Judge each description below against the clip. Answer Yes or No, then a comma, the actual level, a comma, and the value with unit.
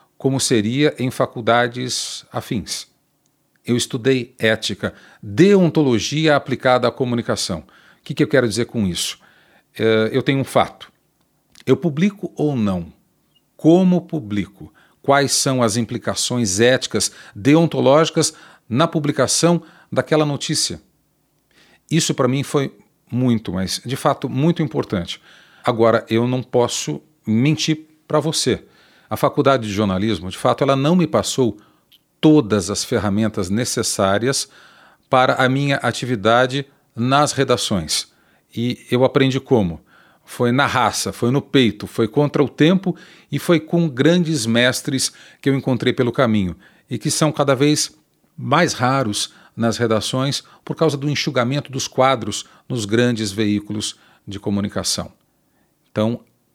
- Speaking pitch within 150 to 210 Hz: No, low, 130 Hz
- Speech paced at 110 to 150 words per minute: Yes, average, 130 wpm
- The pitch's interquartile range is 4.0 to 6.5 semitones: Yes, average, 4.6 semitones